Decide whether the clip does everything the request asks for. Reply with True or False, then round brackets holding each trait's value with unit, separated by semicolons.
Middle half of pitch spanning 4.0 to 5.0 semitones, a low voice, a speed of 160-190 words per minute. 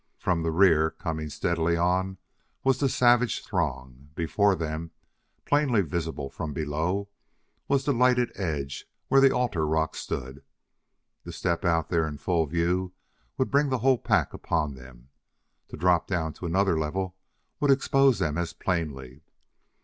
False (4.7 semitones; 85 Hz; 150 wpm)